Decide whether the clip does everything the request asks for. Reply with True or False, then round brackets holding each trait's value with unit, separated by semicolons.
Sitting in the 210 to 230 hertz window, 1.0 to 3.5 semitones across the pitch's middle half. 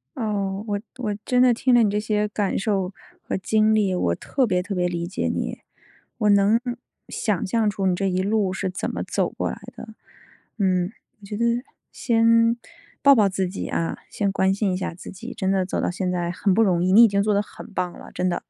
False (200 Hz; 2.7 semitones)